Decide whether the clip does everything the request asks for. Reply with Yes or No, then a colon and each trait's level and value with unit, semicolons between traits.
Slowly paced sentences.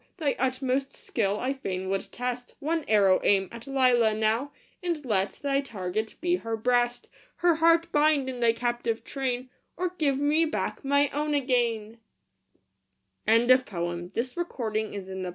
No: average, 155 wpm